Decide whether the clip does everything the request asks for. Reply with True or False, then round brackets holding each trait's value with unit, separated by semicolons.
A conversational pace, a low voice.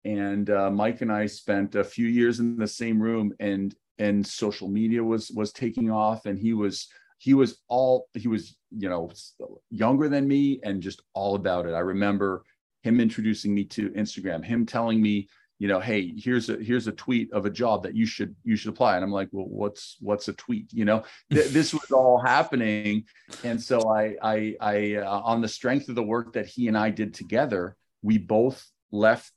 False (210 wpm; 110 Hz)